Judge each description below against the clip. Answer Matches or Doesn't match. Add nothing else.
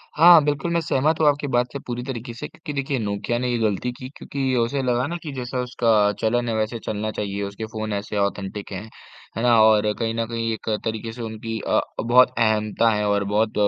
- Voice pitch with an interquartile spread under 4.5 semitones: Matches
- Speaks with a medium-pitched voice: Doesn't match